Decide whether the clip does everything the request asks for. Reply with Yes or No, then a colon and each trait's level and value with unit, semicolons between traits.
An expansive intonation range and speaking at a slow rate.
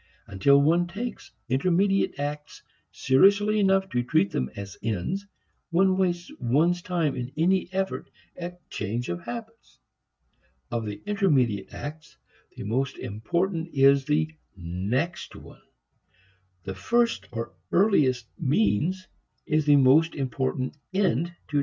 Yes: wide, 7.0 semitones; slow, 130 wpm